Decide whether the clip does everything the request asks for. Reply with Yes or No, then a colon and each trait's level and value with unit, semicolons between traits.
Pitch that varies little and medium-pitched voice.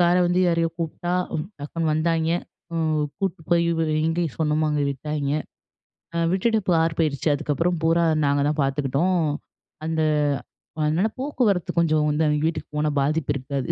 Yes: narrow, 2.2 semitones; medium, 160 Hz